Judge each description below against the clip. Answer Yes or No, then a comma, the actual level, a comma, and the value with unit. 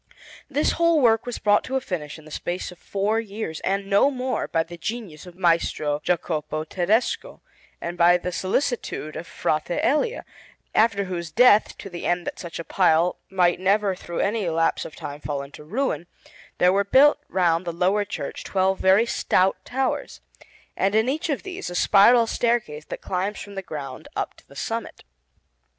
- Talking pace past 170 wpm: Yes, average, 185 wpm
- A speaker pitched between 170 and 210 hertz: Yes, high, 190 Hz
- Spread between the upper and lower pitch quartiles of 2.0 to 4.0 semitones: No, average, 4.7 semitones